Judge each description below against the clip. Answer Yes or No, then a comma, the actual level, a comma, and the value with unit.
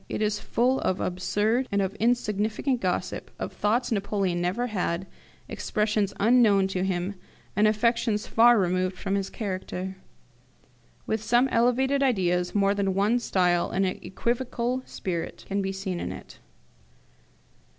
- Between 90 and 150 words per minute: Yes, average, 140 wpm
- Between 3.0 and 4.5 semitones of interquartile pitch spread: Yes, average, 3.7 semitones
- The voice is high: Yes, high, 205 Hz